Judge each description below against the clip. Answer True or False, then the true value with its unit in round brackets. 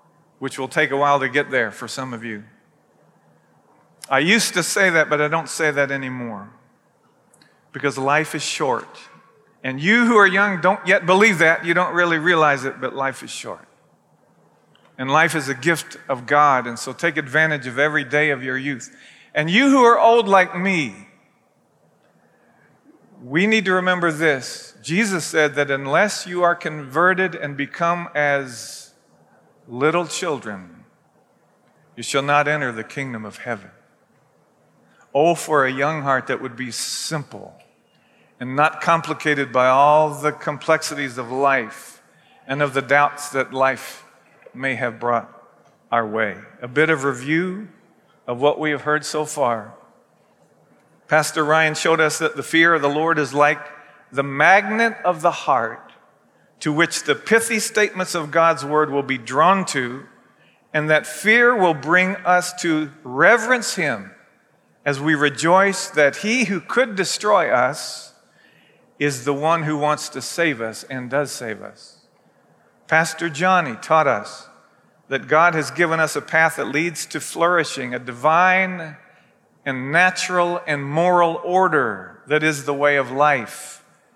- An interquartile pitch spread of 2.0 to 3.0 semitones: False (3.8 semitones)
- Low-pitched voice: False (150 Hz)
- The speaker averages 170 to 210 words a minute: False (160 wpm)